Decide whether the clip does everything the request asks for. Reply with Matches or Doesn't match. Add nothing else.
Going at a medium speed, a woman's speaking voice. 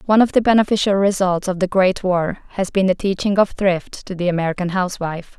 Doesn't match